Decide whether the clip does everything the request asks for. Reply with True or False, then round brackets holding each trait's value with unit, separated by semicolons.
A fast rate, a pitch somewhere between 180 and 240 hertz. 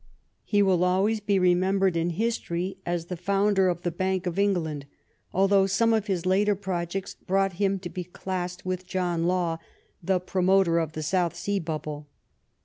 False (175 wpm; 185 Hz)